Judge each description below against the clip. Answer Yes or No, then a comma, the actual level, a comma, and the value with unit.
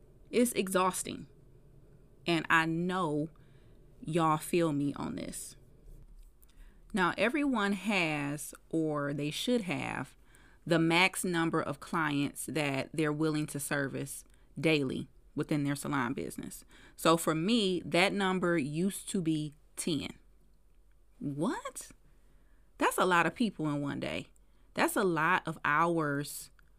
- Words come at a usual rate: No, slow, 125 wpm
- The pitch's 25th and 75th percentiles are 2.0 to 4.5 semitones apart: Yes, average, 3.9 semitones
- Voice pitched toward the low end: No, medium, 160 Hz